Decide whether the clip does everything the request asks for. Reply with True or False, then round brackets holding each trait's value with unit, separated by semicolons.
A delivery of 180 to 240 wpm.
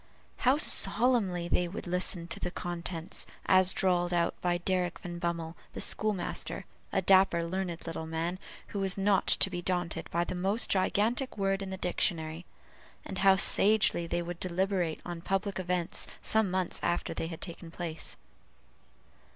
False (165 wpm)